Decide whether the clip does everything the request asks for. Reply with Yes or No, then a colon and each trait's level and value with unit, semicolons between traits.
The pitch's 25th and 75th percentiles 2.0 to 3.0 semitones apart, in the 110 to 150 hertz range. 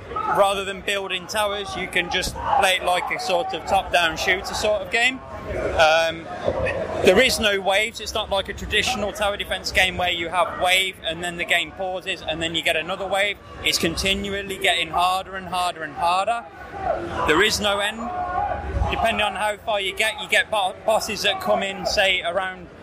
No: narrow, 2.5 semitones; high, 195 Hz